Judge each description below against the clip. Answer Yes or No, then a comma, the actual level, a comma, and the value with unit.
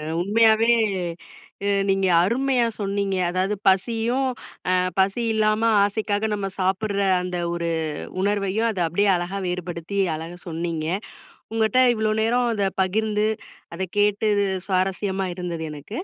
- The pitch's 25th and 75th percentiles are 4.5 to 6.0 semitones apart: No, average, 3.0 semitones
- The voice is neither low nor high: No, high, 200 Hz